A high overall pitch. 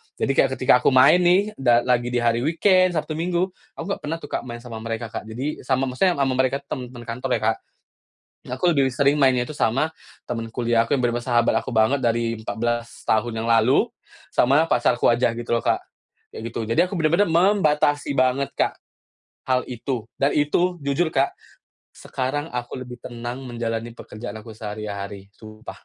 No: low, 125 Hz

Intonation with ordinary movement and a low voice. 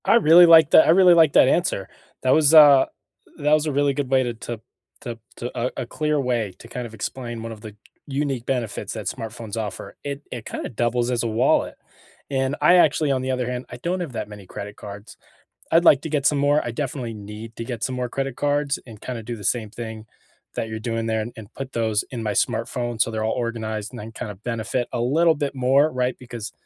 Yes: average, 4.0 semitones; low, 125 Hz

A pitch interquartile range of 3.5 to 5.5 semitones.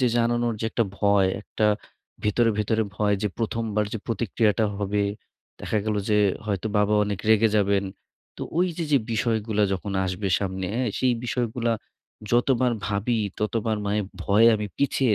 No: narrow, 2.4 semitones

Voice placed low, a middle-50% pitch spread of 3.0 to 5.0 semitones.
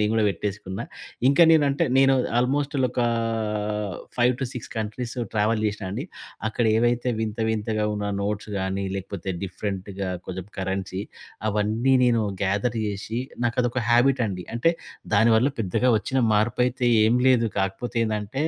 Yes: low, 110 Hz; average, 3.3 semitones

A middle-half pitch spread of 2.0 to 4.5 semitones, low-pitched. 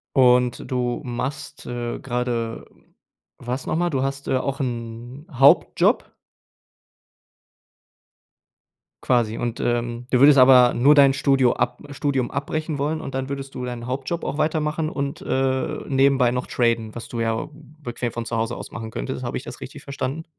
Yes: narrow, 2.5 semitones; low, 130 Hz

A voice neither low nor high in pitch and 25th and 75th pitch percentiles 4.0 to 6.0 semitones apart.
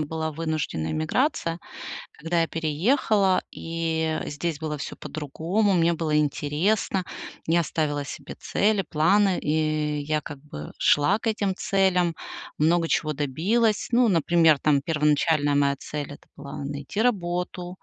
No: medium, 160 Hz; average, 3.3 semitones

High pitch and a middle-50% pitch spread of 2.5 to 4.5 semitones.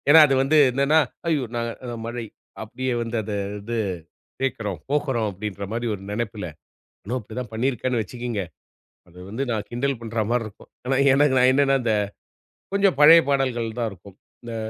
No: low, 120 Hz; average, 3.5 semitones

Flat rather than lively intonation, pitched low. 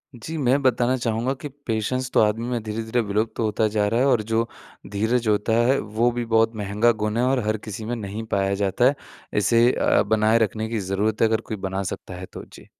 Yes: narrow, 2.1 semitones; low, 110 Hz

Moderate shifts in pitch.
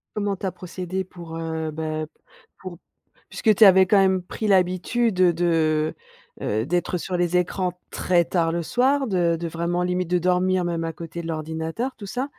No: narrow, 2.3 semitones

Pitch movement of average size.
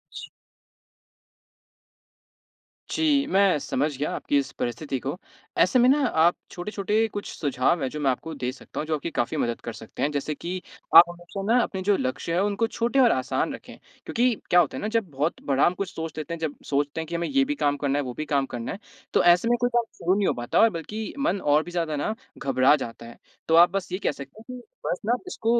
No: wide, 6.5 semitones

